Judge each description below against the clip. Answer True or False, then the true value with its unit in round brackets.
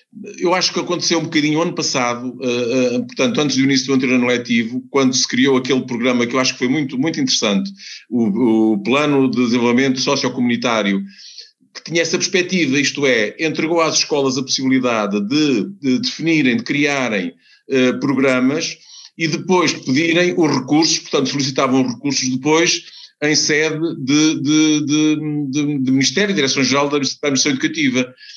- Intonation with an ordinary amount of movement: True (4.2 semitones)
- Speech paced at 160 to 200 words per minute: True (165 wpm)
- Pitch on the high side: False (145 Hz)